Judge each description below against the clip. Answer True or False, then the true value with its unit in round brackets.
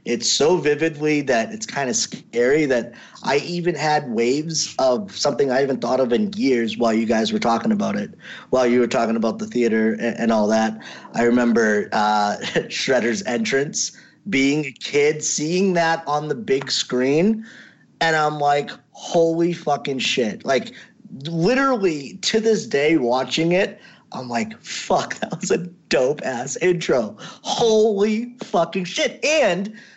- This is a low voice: False (150 Hz)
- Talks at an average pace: True (155 wpm)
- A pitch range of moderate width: False (7.1 semitones)